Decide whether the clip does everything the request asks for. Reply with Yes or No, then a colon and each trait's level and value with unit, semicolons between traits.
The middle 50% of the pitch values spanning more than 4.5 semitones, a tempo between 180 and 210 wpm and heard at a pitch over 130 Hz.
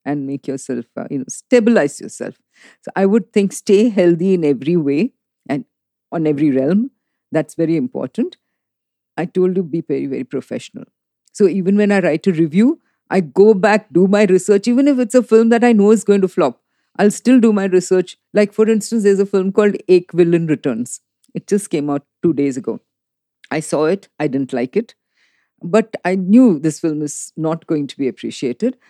Yes: wide, 5.4 semitones; average, 195 wpm; high, 190 Hz